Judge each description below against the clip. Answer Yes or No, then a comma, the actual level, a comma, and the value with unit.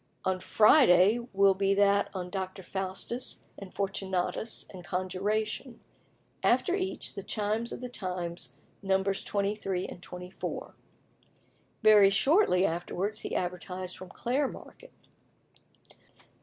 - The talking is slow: Yes, slow, 115 wpm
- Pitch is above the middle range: Yes, high, 195 Hz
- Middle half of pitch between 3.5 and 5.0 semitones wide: No, average, 2.7 semitones